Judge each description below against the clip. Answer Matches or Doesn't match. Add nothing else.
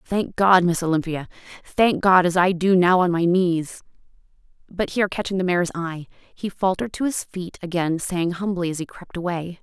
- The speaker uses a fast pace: Doesn't match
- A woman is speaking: Matches